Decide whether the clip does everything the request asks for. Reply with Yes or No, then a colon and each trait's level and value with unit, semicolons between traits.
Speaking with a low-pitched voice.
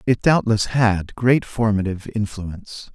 Yes: low, 110 Hz